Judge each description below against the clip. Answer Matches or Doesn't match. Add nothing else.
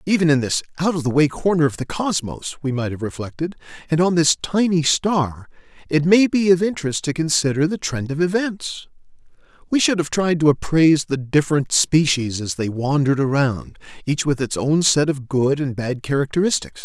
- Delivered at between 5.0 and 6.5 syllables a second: Matches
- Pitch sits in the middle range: Matches